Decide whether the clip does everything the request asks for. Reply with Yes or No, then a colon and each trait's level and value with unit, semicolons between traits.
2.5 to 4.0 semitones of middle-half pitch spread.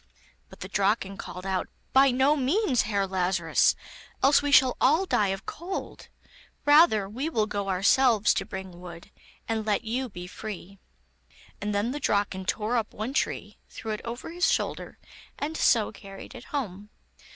No: average, 5.3 semitones